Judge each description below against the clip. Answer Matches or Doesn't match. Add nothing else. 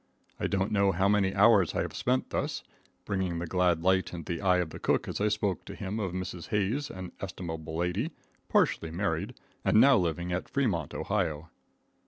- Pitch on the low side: Matches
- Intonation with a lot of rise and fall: Doesn't match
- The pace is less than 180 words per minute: Doesn't match